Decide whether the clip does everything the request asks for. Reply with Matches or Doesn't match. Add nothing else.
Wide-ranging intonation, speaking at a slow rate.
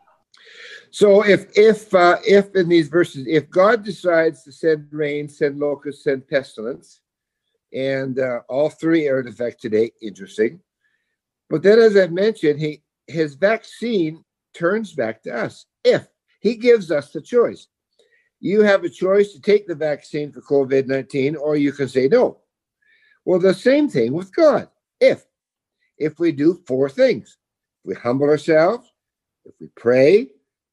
Doesn't match